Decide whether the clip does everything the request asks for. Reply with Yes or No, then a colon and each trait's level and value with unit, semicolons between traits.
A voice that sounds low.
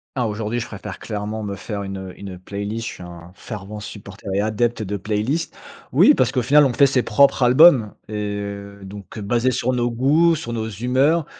Yes: low, 110 Hz